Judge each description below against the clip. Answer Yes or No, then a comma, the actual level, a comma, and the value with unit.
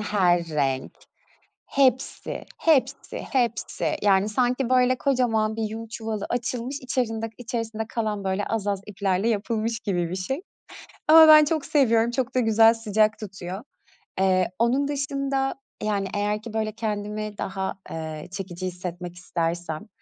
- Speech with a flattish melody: No, average, 4.2 semitones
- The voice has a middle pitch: No, high, 220 Hz